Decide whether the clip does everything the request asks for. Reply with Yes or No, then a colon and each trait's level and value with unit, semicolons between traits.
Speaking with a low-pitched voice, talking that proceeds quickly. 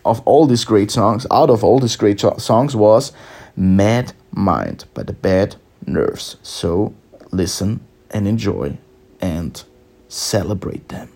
No: low, 105 Hz; slow, 135 wpm